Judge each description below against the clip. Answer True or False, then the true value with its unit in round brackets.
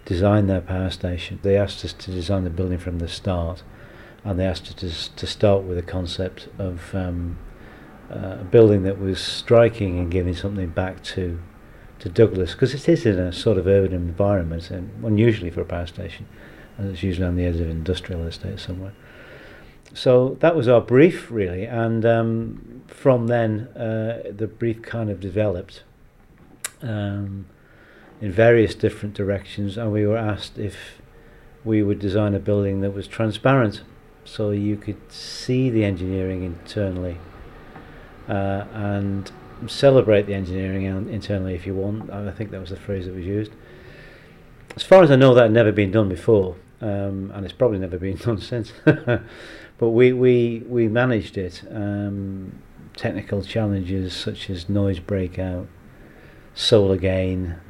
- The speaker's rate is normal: True (165 wpm)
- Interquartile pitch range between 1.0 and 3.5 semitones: True (3.2 semitones)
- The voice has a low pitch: True (100 Hz)